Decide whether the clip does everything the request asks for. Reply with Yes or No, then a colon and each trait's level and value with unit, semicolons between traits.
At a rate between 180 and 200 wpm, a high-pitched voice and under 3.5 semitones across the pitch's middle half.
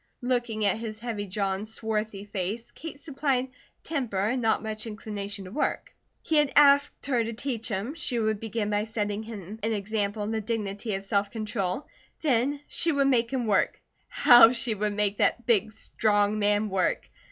Yes: average, 185 wpm; high, 220 Hz; average, 2.8 semitones